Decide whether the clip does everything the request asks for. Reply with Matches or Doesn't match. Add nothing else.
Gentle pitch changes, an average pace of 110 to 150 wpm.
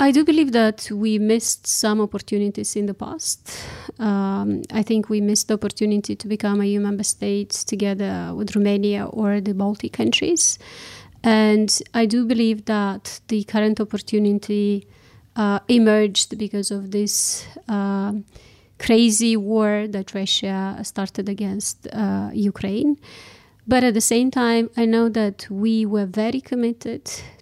Matches